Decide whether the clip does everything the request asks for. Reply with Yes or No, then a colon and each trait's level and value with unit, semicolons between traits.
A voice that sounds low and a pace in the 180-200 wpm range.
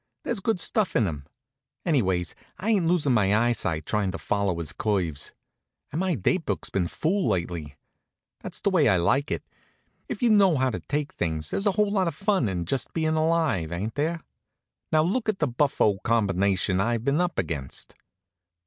Yes: low, 125 Hz; average, 185 wpm